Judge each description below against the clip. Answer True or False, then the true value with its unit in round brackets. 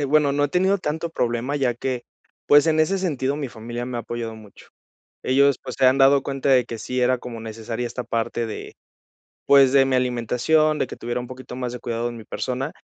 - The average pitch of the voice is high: False (130 Hz)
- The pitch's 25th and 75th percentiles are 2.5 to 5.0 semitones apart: True (2.9 semitones)